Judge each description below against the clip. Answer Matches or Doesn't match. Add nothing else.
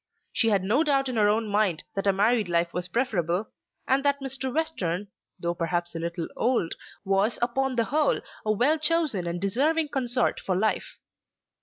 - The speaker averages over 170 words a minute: Matches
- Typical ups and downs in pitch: Doesn't match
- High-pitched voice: Matches